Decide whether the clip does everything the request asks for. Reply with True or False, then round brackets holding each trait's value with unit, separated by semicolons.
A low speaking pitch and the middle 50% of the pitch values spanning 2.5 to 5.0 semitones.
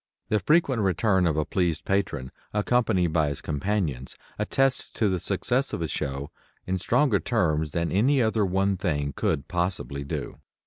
False (90 Hz; 5.5 semitones)